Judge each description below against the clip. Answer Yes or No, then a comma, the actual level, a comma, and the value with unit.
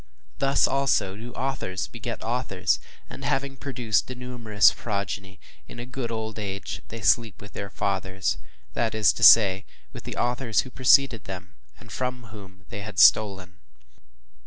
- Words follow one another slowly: No, average, 160 wpm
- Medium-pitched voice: No, low, 110 Hz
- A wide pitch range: No, average, 3.9 semitones